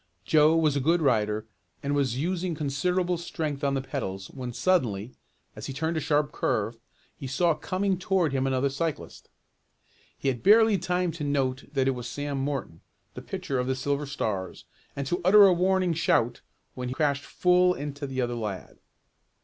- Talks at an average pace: Yes, average, 180 wpm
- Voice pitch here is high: No, medium, 145 Hz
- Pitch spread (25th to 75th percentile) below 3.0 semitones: No, average, 4.7 semitones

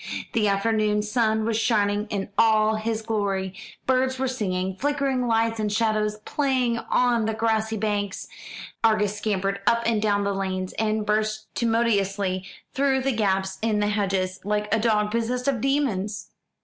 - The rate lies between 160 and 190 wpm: No, average, 150 wpm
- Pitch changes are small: Yes, narrow, 2.1 semitones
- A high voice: Yes, high, 215 Hz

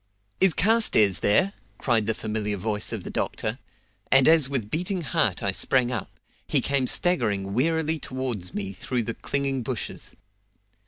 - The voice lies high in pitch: No, low, 125 Hz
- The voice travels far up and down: Yes, wide, 6.8 semitones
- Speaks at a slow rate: No, average, 155 wpm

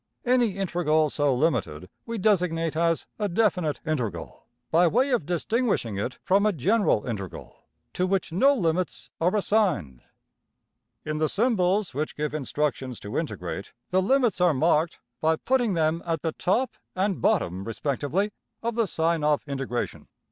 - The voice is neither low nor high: Yes, medium, 165 Hz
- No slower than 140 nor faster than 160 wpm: Yes, average, 150 wpm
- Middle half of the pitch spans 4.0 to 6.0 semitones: Yes, wide, 5.6 semitones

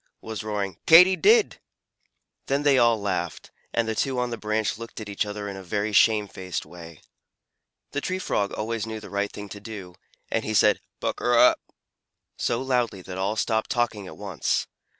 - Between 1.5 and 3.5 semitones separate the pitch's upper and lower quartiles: Yes, average, 2.8 semitones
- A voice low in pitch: Yes, low, 110 Hz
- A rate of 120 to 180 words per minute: No, average, 190 wpm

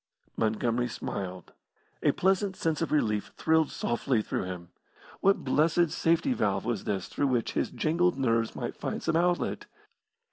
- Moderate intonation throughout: No, wide, 7.4 semitones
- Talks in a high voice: No, low, 135 Hz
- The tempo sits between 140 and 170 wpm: Yes, average, 150 wpm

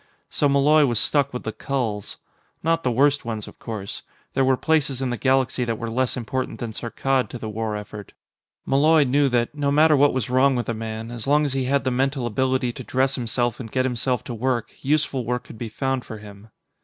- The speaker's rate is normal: No, fast, 225 wpm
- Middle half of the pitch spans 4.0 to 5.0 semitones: No, average, 2.9 semitones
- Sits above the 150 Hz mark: No, low, 130 Hz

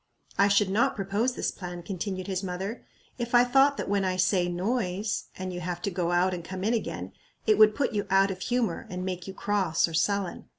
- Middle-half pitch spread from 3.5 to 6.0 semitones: No, average, 2.7 semitones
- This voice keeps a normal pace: No, fast, 225 wpm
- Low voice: No, high, 195 Hz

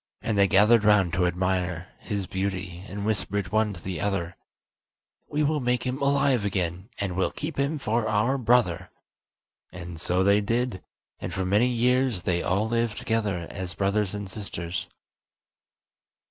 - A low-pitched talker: Yes, low, 100 Hz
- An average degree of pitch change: Yes, average, 4.1 semitones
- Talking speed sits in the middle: Yes, average, 160 wpm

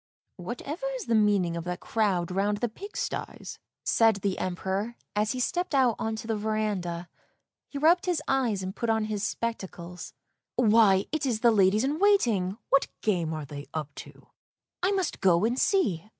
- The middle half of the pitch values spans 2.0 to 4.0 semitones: No, average, 5.1 semitones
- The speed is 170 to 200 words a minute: Yes, average, 195 wpm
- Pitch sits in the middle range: No, high, 215 Hz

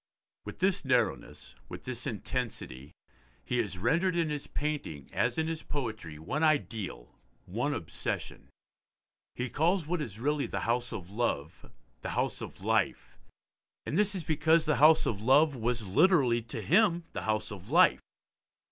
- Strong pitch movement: Yes, wide, 6.5 semitones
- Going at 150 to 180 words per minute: Yes, average, 155 wpm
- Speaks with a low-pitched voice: Yes, low, 125 Hz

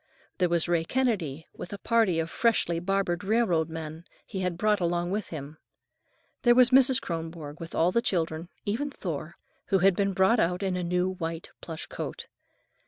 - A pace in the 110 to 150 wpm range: No, average, 180 wpm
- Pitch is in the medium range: Yes, medium, 180 Hz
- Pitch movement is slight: No, average, 3.6 semitones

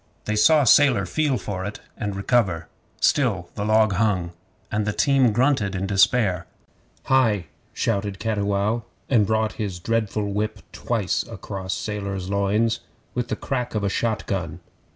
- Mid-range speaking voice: No, low, 105 Hz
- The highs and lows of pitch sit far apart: No, average, 2.7 semitones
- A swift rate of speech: No, average, 150 wpm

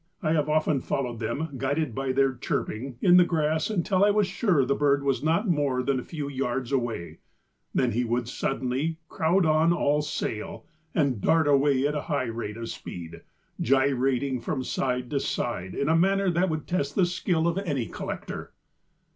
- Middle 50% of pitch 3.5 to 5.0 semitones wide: Yes, average, 4.2 semitones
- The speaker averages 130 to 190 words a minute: Yes, average, 185 wpm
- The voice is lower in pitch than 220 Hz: Yes, medium, 140 Hz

